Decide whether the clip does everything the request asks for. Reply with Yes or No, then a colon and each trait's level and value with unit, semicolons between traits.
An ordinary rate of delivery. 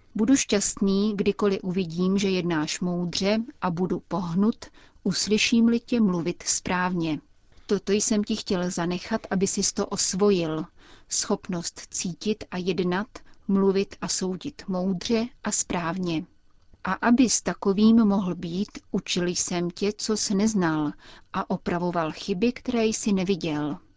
Yes: average, 130 wpm